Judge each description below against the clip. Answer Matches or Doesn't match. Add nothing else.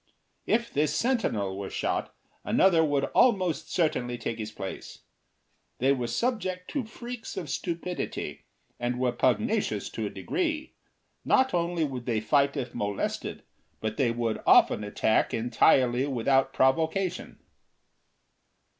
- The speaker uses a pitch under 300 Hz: Matches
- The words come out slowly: Matches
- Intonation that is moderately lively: Doesn't match